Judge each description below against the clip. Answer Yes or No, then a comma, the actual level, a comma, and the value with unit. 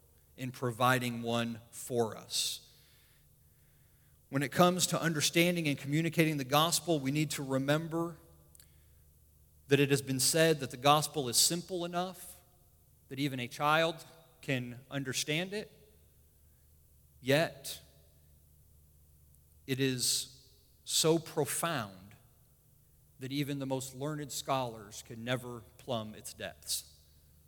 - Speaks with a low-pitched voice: Yes, low, 130 Hz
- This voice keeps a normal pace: No, slow, 115 wpm